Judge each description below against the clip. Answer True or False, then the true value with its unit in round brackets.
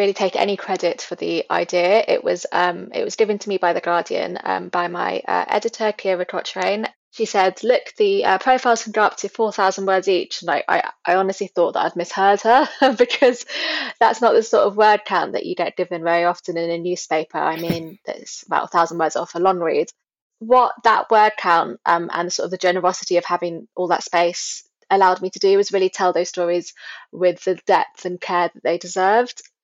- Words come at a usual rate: False (220 wpm)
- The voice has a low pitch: False (185 Hz)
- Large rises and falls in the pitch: False (3.4 semitones)